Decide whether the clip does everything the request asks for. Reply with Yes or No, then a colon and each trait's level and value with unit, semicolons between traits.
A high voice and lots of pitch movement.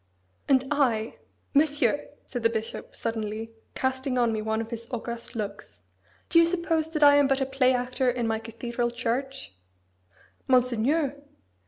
No: very high, 250 Hz; average, 3.2 semitones